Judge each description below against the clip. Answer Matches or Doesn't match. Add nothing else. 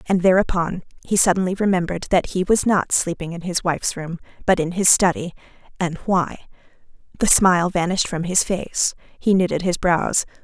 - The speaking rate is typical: Matches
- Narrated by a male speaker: Doesn't match